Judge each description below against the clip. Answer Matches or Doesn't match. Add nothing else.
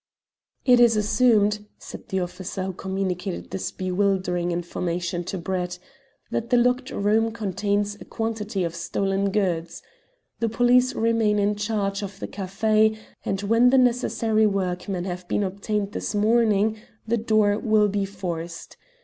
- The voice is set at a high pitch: Matches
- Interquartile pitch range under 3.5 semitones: Matches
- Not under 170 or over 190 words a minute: Doesn't match